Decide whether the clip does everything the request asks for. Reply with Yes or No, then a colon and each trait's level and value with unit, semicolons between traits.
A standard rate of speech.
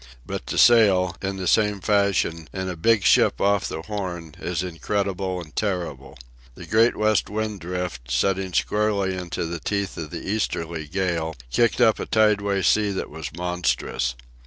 Yes: average, 165 wpm